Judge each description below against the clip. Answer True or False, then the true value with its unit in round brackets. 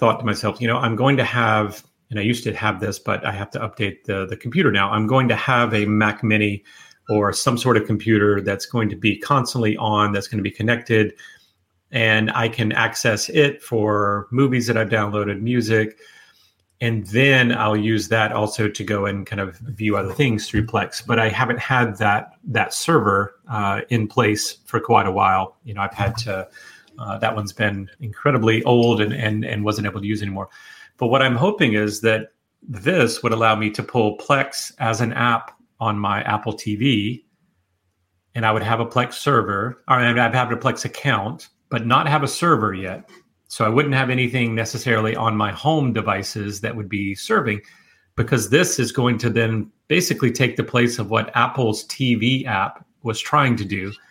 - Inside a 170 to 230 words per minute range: True (200 wpm)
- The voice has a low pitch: True (110 Hz)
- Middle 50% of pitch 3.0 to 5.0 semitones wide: False (2.6 semitones)